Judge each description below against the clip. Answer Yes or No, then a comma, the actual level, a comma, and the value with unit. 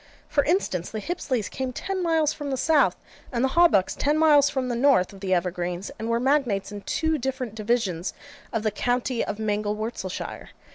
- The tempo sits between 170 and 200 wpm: Yes, average, 185 wpm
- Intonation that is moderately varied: No, wide, 5.7 semitones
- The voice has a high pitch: Yes, high, 245 Hz